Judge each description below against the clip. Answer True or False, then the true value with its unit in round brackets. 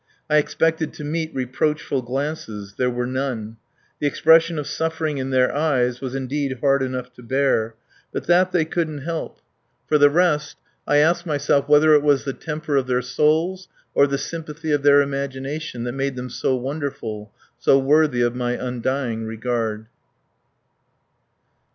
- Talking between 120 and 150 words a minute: False (160 wpm)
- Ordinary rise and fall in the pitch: True (3.4 semitones)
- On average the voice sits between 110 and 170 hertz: True (140 Hz)